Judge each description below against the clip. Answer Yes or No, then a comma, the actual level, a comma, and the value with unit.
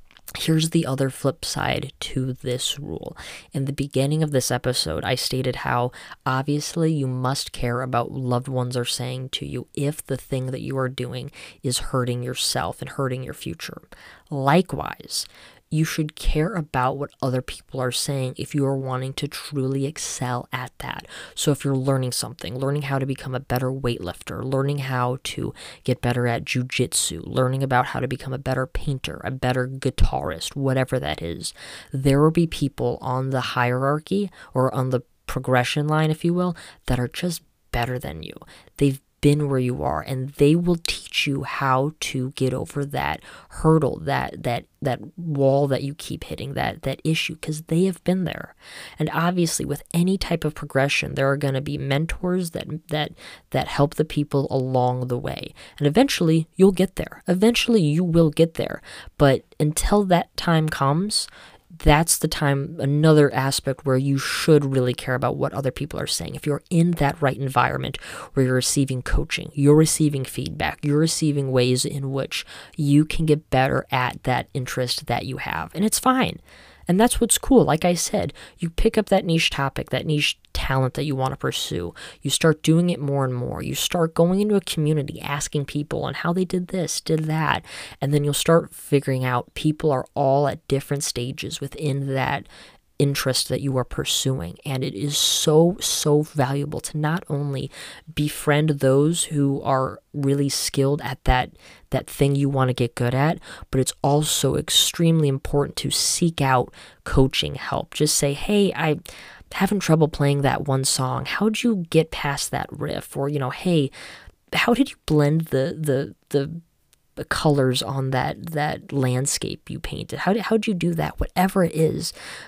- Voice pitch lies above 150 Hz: No, medium, 140 Hz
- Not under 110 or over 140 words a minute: No, average, 180 wpm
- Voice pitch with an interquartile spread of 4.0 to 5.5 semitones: No, average, 3.2 semitones